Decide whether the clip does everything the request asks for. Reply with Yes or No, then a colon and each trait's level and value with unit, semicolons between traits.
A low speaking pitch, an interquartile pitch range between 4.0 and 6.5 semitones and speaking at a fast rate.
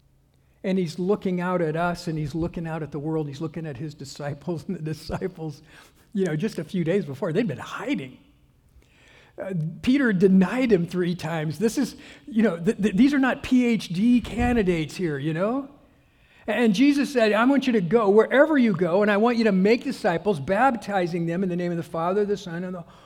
No: high, 190 Hz; average, 5.1 semitones; fast, 215 wpm